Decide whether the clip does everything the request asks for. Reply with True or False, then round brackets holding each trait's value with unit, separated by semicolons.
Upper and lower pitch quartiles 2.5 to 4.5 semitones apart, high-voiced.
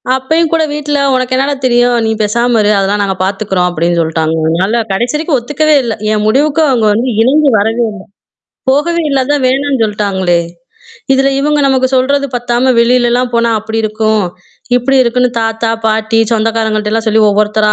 True (3.9 semitones; 235 Hz)